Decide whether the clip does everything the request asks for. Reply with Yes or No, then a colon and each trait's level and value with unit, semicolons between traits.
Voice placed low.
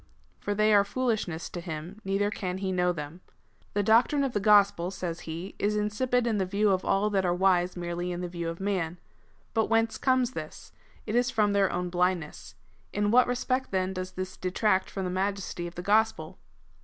No: high, 195 Hz